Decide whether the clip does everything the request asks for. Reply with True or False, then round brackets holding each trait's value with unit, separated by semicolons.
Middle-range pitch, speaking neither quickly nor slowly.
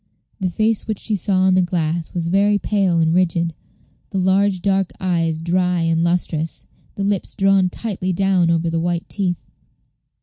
True (180 Hz; 170 wpm)